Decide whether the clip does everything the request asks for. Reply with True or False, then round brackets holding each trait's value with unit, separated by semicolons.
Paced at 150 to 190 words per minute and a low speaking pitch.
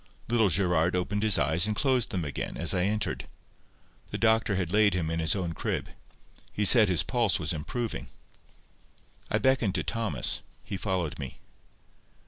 True (165 wpm; 95 Hz)